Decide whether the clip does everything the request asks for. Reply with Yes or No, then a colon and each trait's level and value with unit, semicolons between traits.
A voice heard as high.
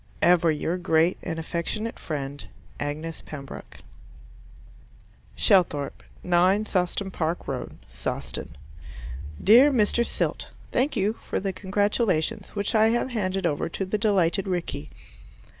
No: medium, 180 Hz